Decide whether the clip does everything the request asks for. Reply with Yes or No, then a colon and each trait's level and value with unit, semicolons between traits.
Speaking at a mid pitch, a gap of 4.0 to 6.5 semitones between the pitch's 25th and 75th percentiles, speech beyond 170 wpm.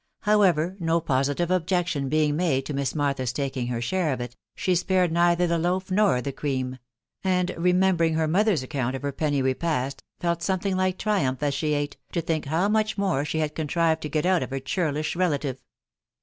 Yes: medium, 160 Hz; average, 4.5 semitones; average, 200 wpm